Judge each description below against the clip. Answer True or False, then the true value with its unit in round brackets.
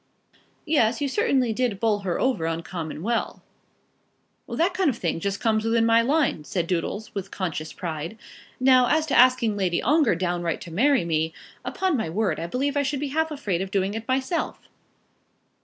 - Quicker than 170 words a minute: True (180 wpm)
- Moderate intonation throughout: False (7.1 semitones)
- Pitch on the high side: True (225 Hz)